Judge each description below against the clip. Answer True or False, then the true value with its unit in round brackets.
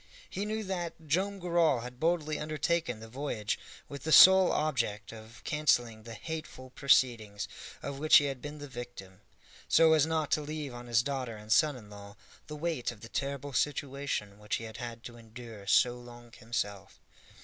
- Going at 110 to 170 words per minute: False (180 wpm)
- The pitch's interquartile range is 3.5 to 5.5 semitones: True (5.0 semitones)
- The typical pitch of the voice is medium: False (130 Hz)